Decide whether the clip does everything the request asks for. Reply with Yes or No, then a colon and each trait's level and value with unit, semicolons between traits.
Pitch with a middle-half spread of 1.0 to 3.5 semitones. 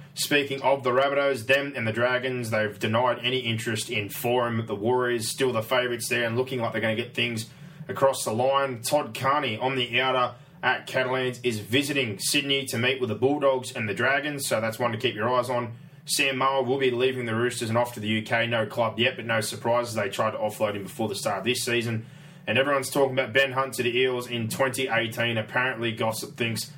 Yes: narrow, 2.5 semitones